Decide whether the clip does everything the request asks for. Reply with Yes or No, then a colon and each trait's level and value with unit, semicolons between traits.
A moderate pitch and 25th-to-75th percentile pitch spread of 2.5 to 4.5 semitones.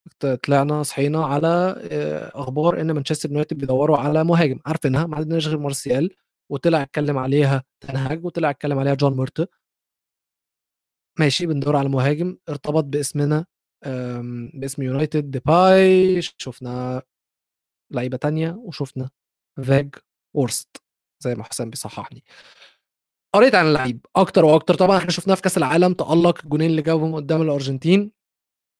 Yes: medium, 150 Hz; average, 3.2 semitones